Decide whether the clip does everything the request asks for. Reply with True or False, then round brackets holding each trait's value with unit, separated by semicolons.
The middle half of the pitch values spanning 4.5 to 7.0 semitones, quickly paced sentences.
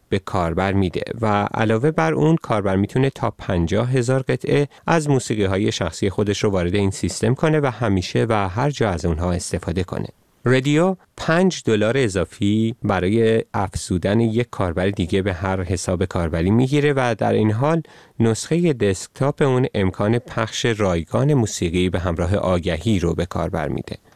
True (5.3 semitones; 160 wpm)